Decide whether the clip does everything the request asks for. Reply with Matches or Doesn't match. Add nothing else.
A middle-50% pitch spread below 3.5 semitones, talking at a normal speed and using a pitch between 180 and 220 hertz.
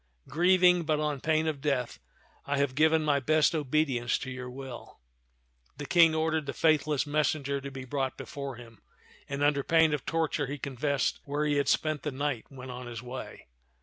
Doesn't match